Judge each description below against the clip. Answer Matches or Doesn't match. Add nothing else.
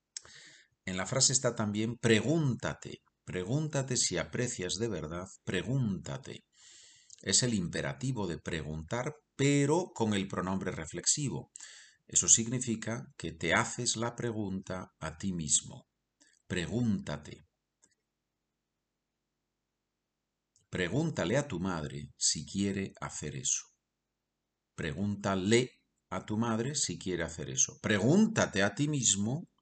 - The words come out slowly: Matches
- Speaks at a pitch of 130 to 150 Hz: Doesn't match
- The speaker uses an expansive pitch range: Matches